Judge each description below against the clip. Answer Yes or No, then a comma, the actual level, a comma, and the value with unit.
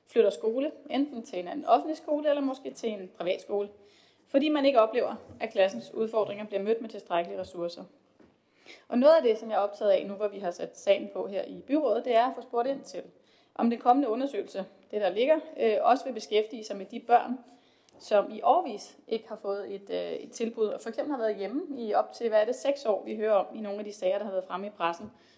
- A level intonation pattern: No, average, 4.7 semitones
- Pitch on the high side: Yes, high, 225 Hz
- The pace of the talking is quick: Yes, fast, 240 wpm